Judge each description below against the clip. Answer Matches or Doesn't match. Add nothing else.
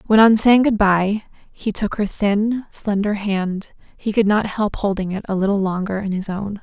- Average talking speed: Doesn't match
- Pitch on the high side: Matches